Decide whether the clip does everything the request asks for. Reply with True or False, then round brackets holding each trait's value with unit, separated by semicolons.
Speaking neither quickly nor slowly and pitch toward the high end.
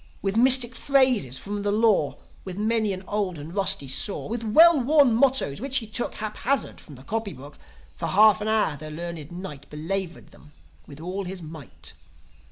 True (180 wpm; 200 Hz)